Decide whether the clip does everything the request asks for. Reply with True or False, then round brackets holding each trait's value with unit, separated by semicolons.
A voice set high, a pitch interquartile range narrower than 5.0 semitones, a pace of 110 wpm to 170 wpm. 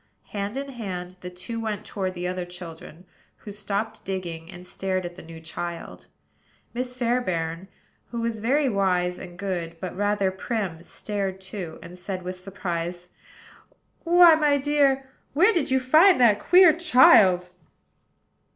False (195 Hz; 5.4 semitones; 150 wpm)